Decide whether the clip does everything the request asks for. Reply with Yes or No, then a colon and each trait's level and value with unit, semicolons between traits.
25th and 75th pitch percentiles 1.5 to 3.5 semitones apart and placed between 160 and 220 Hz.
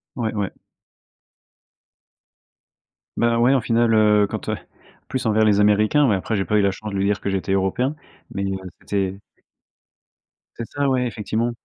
No: average, 3.0 semitones; low, 105 Hz